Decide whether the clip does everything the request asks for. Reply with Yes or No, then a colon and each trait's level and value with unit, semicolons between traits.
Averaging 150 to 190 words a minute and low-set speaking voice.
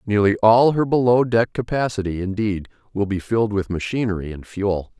Yes: average, 170 wpm; low, 105 Hz